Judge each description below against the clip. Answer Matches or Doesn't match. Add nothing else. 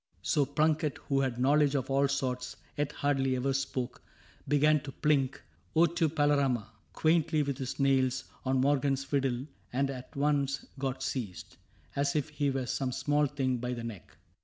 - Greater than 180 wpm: Doesn't match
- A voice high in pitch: Doesn't match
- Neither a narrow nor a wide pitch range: Doesn't match